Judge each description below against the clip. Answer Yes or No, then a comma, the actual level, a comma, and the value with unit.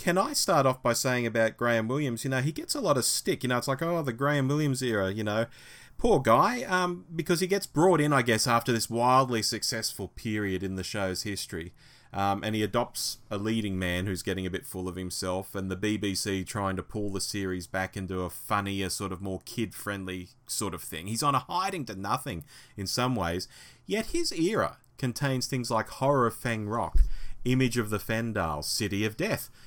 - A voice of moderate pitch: No, low, 110 Hz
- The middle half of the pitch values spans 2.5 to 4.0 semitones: No, average, 4.8 semitones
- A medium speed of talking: No, fast, 215 wpm